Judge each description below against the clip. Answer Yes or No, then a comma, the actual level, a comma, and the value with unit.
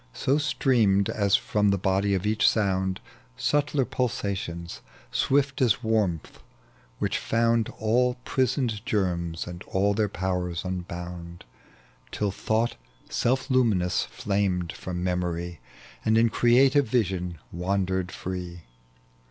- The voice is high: No, low, 100 Hz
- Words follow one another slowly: Yes, slow, 115 wpm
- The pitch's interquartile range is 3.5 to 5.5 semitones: Yes, average, 4.6 semitones